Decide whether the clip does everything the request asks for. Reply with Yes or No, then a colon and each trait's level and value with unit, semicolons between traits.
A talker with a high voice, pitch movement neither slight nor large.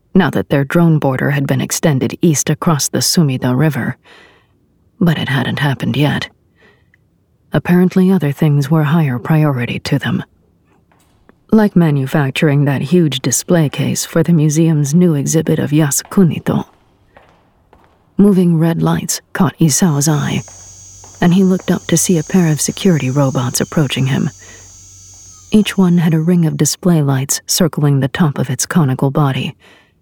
No: medium, 155 Hz; average, 4.2 semitones